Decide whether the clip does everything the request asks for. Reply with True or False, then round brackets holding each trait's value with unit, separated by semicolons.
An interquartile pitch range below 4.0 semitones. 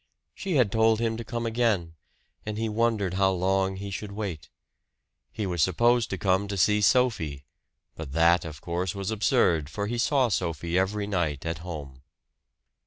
False (4.6 semitones)